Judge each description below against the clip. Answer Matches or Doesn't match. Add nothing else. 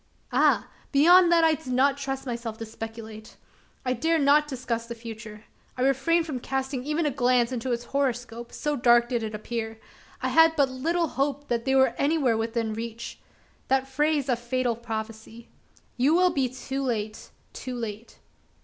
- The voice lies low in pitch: Doesn't match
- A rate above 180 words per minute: Doesn't match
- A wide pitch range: Doesn't match